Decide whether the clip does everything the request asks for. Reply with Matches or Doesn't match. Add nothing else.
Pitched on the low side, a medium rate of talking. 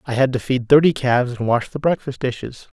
Doesn't match